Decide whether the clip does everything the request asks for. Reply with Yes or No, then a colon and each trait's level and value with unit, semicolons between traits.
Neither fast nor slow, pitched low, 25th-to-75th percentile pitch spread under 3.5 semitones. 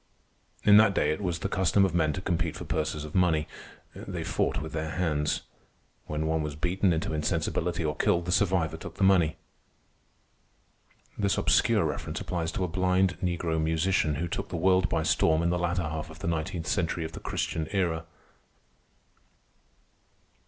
Yes: average, 175 wpm; very low, 85 Hz; narrow, 2.6 semitones